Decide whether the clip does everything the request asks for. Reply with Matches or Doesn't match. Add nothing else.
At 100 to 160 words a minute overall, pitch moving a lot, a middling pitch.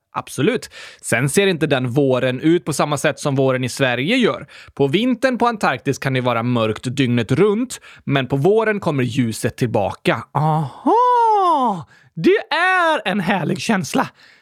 Matches